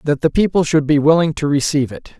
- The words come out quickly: Yes, fast, 245 wpm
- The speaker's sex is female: No, male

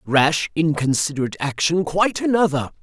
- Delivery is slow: Yes, slow, 105 wpm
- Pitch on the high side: No, medium, 160 Hz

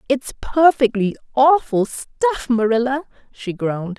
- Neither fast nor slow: No, slow, 105 wpm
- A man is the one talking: No, female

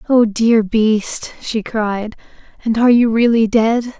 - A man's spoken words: No, female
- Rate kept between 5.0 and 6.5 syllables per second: No, 3.9 syllables/s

